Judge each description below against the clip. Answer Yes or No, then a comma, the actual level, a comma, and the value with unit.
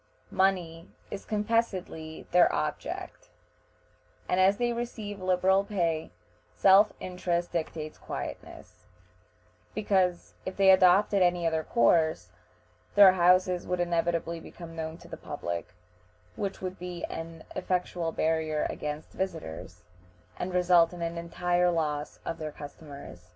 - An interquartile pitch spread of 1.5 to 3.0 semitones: Yes, narrow, 2.5 semitones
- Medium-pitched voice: Yes, medium, 175 Hz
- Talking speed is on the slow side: Yes, slow, 125 wpm